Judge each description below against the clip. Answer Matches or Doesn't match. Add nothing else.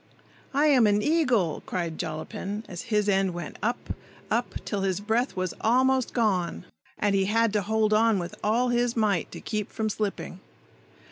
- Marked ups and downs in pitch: Doesn't match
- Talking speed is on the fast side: Doesn't match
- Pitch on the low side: Doesn't match